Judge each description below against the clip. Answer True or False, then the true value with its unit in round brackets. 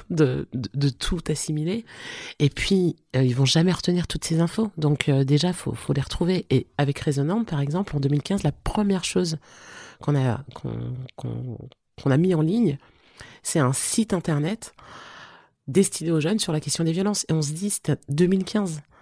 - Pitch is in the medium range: True (155 Hz)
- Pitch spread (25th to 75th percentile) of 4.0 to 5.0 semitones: True (4.7 semitones)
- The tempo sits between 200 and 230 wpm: False (190 wpm)